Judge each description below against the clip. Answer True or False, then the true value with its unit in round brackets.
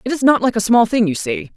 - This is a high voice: True (220 Hz)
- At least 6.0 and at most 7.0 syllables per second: True (6.3 syllables/s)